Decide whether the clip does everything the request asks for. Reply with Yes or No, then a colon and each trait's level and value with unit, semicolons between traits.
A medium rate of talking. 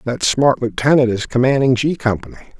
Yes: average, 160 wpm